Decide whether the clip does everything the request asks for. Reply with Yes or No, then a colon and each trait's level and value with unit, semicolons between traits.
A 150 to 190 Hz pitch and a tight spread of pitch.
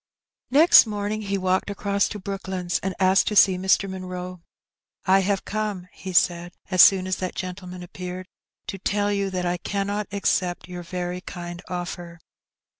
Yes: medium, 185 Hz; narrow, 1.8 semitones